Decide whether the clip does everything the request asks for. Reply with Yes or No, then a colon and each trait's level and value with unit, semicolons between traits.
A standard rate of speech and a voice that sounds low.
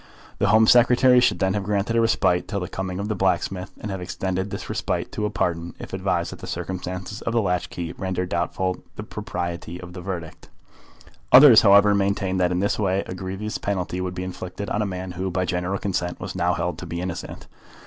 No: fast, 220 wpm; very low, 95 Hz